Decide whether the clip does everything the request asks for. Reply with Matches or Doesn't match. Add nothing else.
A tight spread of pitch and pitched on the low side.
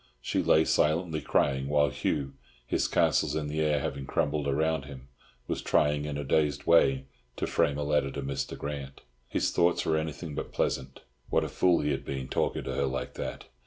Matches